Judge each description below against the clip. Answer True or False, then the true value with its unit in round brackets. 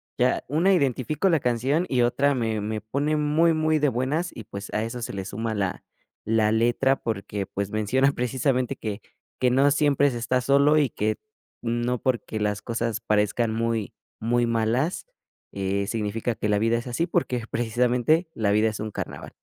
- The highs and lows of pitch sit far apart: False (4.1 semitones)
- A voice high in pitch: False (120 Hz)